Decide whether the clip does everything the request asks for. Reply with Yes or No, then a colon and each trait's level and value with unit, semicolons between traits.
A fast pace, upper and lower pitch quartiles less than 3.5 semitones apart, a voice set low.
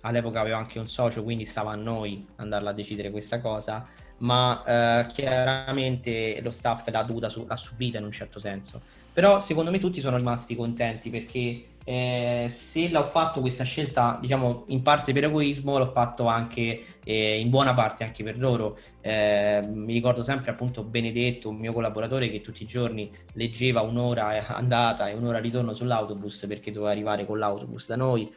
Yes: fast, 175 wpm; narrow, 2.5 semitones; low, 115 Hz